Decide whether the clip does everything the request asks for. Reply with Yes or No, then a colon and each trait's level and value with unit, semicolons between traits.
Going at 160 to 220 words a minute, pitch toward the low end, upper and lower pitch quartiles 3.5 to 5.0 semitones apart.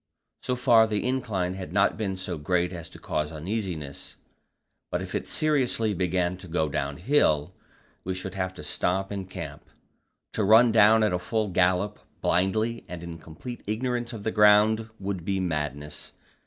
Yes: average, 165 wpm; very low, 95 Hz; average, 4.0 semitones